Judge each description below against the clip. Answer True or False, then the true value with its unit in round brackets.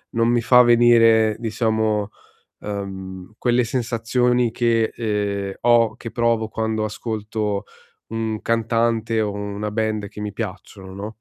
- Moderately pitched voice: False (110 Hz)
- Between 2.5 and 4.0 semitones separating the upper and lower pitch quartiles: False (1.9 semitones)